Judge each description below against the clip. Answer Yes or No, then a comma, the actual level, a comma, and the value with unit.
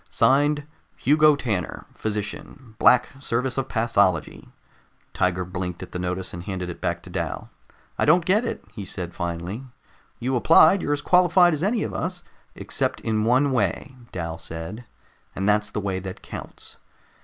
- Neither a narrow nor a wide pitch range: No, wide, 8.1 semitones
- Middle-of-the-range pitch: No, low, 110 Hz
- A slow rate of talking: No, average, 165 wpm